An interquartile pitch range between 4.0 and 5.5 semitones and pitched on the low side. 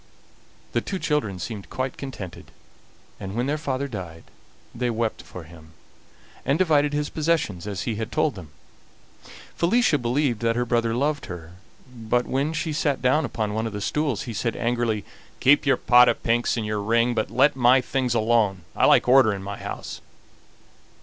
Yes: average, 4.7 semitones; low, 120 Hz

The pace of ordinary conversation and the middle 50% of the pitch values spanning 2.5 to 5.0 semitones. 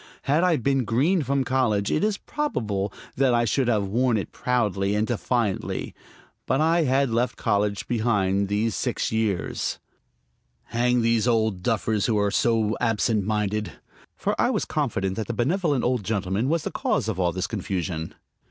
Yes: average, 170 wpm; average, 3.8 semitones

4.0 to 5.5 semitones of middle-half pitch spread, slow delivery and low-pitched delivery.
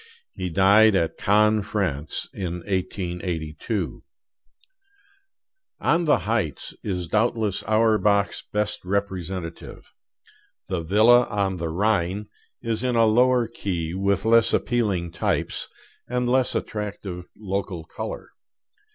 No: average, 3.6 semitones; slow, 110 wpm; low, 100 Hz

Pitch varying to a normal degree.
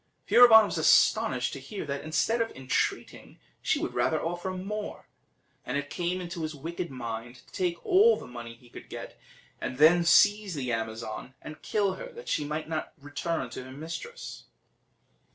No: wide, 6.6 semitones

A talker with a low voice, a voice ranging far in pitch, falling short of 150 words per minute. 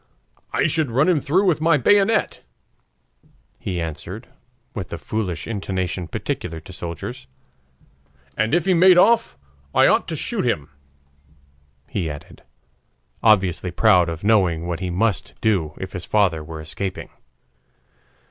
Yes: very low, 95 Hz; wide, 7.3 semitones; average, 140 wpm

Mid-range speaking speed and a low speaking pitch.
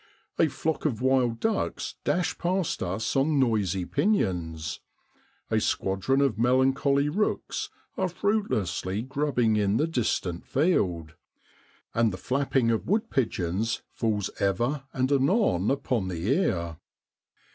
No: slow, 125 wpm; low, 125 Hz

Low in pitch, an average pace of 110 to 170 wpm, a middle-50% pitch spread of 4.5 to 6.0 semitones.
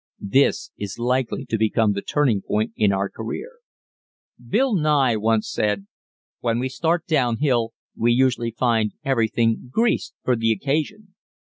No: low, 120 Hz; average, 145 wpm; average, 4.0 semitones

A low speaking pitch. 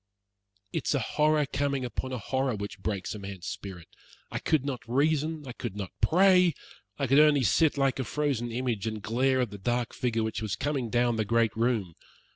Yes: low, 125 Hz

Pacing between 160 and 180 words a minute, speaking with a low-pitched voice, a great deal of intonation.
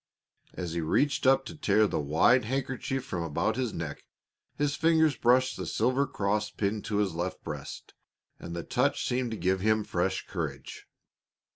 Yes: average, 170 wpm; low, 110 Hz; wide, 6.1 semitones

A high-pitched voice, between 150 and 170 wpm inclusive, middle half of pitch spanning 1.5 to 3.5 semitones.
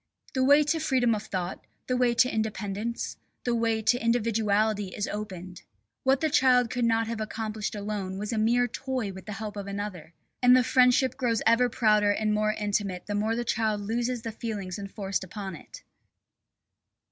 No: high, 220 Hz; average, 180 wpm; average, 2.8 semitones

